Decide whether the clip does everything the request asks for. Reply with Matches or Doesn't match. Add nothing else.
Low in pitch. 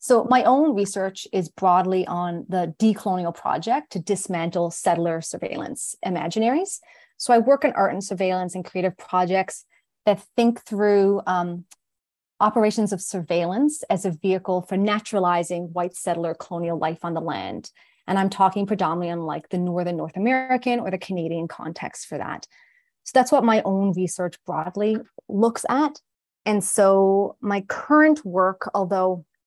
Doesn't match